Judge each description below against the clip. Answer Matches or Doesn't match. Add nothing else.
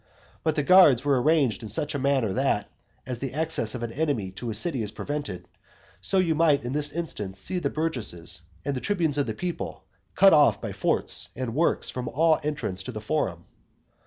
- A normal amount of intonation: Doesn't match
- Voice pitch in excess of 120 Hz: Matches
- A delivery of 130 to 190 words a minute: Doesn't match